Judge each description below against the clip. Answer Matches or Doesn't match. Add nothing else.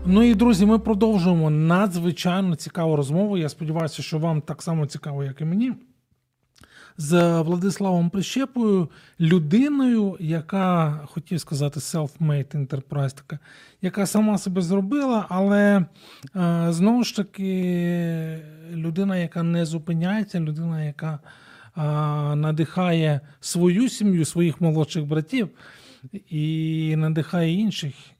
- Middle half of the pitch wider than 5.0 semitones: Doesn't match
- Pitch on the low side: Doesn't match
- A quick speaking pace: Doesn't match